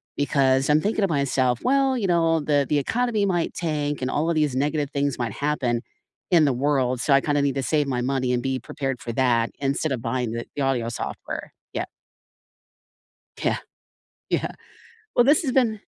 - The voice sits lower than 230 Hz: Yes, medium, 140 Hz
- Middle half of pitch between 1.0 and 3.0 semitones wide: No, average, 3.9 semitones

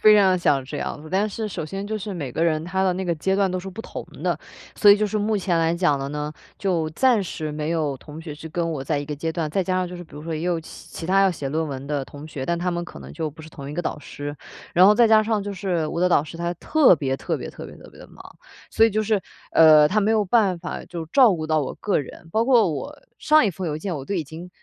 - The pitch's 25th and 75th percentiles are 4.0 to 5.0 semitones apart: Yes, average, 4.3 semitones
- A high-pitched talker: No, medium, 170 Hz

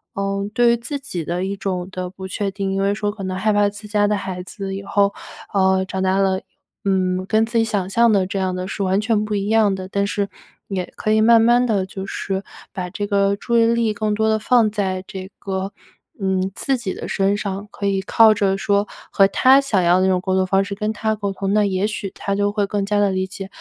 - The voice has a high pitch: Yes, high, 200 Hz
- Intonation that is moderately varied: No, narrow, 1.9 semitones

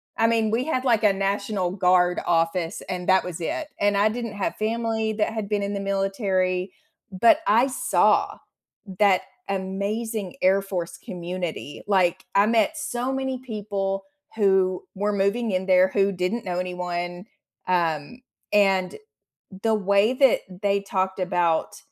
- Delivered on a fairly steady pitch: No, average, 3.0 semitones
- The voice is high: Yes, high, 195 Hz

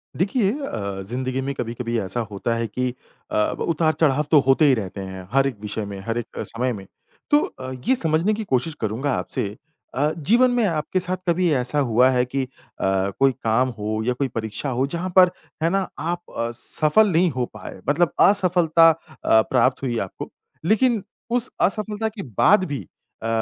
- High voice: No, low, 135 Hz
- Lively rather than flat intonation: Yes, wide, 7.3 semitones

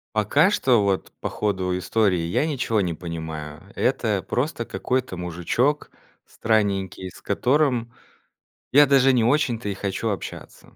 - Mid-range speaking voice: No, low, 105 Hz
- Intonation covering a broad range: Yes, wide, 5.7 semitones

